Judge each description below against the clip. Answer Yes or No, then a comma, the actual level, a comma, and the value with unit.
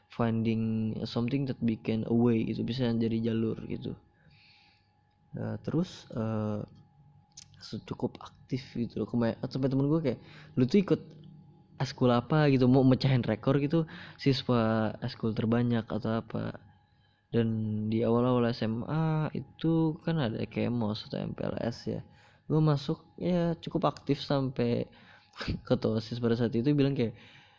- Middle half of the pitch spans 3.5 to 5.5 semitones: Yes, average, 4.2 semitones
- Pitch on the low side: Yes, low, 120 Hz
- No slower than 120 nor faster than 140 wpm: Yes, average, 135 wpm